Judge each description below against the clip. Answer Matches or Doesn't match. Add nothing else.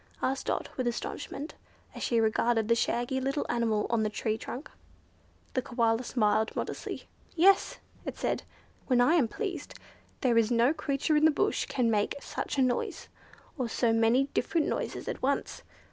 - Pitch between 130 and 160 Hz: Doesn't match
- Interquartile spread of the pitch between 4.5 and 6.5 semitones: Doesn't match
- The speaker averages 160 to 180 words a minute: Matches